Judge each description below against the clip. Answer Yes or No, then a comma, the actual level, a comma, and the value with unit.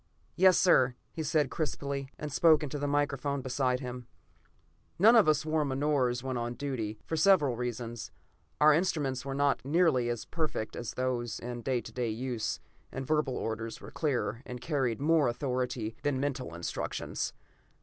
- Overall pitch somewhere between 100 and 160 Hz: Yes, low, 135 Hz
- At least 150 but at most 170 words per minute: Yes, average, 160 wpm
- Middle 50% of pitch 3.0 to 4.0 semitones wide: Yes, average, 3.5 semitones